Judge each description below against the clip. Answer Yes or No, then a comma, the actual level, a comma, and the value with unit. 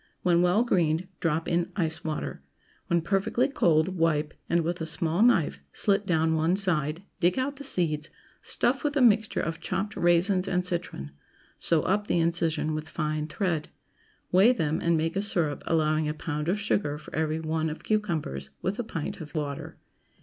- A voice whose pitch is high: No, medium, 170 Hz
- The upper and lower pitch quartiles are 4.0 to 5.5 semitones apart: No, average, 3.3 semitones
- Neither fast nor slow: Yes, average, 180 wpm